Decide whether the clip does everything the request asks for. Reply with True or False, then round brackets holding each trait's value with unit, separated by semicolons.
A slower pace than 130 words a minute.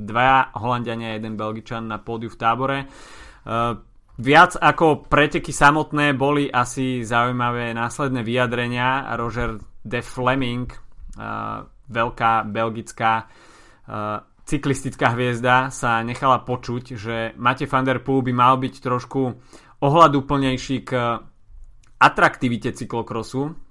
True (110 wpm)